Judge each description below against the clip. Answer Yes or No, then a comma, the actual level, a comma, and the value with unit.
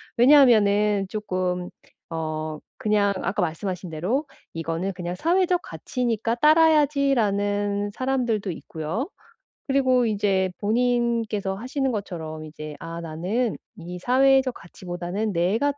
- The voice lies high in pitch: Yes, high, 205 Hz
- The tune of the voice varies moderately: No, wide, 5.8 semitones